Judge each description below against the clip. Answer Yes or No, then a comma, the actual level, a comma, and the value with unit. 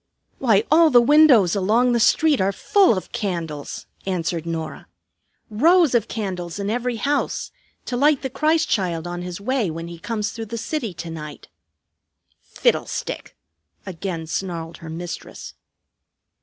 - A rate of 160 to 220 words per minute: No, average, 145 wpm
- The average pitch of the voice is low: No, high, 200 Hz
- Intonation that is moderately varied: No, wide, 6.5 semitones